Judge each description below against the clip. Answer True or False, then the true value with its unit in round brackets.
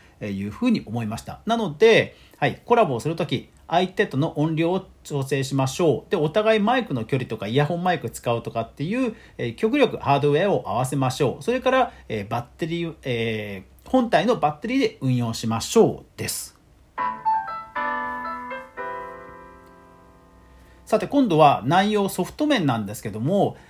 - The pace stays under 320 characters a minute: False (330 characters per minute)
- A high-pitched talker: False (145 Hz)